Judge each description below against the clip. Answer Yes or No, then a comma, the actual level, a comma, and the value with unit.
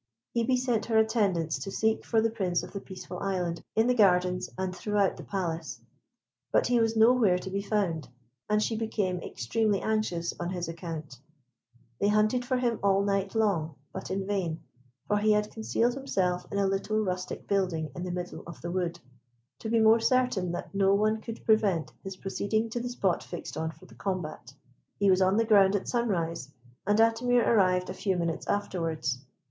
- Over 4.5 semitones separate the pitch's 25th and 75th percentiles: No, average, 3.6 semitones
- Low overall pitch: No, high, 195 Hz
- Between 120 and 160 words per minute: No, average, 190 wpm